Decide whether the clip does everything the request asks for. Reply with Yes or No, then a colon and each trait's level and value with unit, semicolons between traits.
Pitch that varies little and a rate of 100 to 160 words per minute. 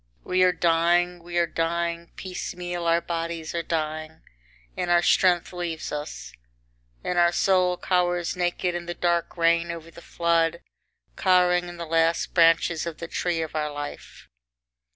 Yes: narrow, 1.2 semitones; average, 155 wpm